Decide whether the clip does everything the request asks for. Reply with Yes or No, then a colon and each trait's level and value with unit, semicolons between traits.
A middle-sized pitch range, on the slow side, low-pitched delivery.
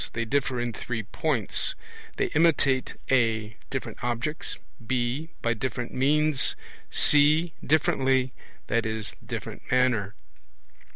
Yes: average, 3.8 semitones; slow, 105 wpm; low, 130 Hz